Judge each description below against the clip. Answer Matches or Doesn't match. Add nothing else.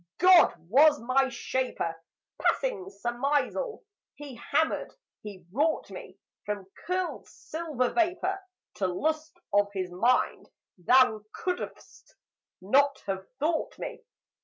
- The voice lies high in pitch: Matches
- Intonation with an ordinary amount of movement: Doesn't match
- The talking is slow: Matches